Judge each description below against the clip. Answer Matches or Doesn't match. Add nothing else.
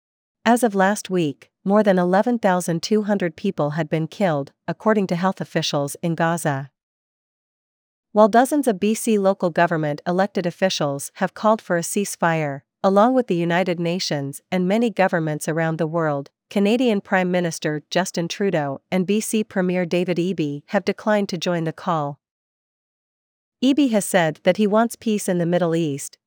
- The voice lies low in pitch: Doesn't match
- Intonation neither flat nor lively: Matches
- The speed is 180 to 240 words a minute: Doesn't match